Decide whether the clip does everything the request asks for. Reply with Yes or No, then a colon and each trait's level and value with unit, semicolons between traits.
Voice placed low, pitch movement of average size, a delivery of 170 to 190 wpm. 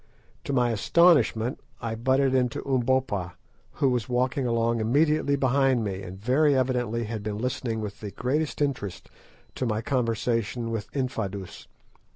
No: low, 120 Hz; average, 3.1 semitones; average, 145 wpm